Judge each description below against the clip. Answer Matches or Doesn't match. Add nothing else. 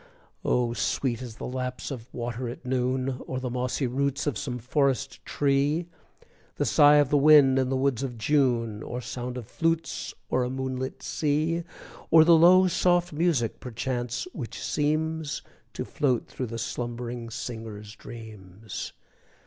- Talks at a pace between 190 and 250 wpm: Doesn't match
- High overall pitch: Doesn't match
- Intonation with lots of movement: Doesn't match